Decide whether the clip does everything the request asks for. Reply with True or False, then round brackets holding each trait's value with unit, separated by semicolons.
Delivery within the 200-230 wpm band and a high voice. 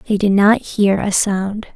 True (205 wpm; 205 Hz)